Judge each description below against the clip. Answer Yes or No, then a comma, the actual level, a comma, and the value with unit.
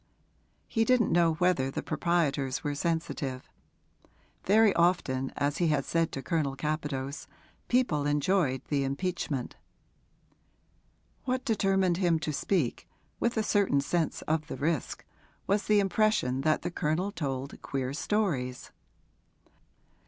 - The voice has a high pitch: No, medium, 160 Hz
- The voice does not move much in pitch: No, wide, 5.5 semitones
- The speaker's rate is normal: No, slow, 125 wpm